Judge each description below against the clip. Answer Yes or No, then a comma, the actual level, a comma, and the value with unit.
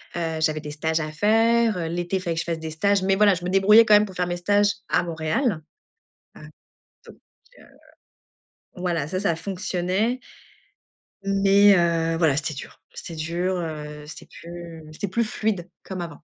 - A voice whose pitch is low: No, medium, 175 Hz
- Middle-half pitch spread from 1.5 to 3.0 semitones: No, average, 3.6 semitones